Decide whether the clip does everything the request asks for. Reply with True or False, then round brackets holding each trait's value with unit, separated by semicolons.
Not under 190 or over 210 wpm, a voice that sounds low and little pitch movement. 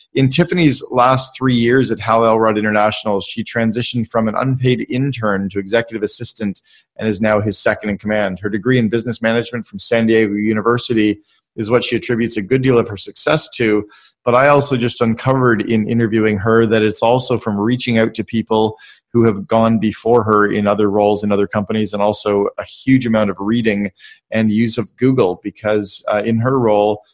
True (195 wpm; 115 Hz; 2.2 semitones)